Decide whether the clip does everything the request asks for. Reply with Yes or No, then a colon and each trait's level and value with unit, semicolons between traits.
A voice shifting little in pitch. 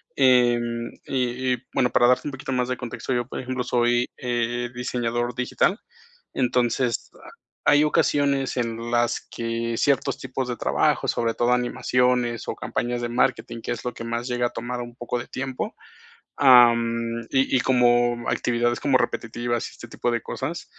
Yes: narrow, 1.2 semitones